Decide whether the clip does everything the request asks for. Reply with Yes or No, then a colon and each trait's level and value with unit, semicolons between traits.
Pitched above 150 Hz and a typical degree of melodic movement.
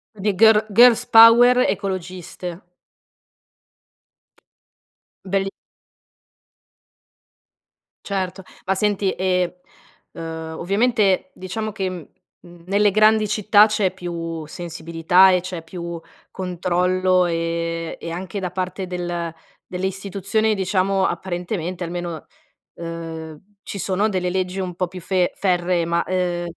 No: medium, 185 Hz; narrow, 2.2 semitones